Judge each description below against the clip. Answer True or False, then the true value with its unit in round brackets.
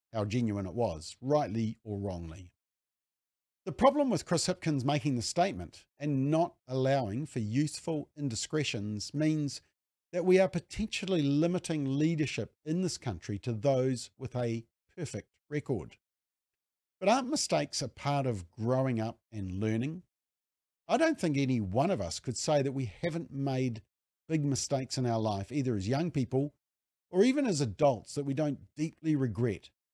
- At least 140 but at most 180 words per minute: True (155 wpm)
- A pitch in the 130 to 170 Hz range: True (135 Hz)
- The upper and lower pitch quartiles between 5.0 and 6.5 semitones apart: True (5.5 semitones)